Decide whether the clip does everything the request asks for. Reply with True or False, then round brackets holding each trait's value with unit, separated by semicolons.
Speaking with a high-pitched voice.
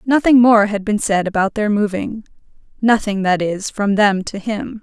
True (210 Hz)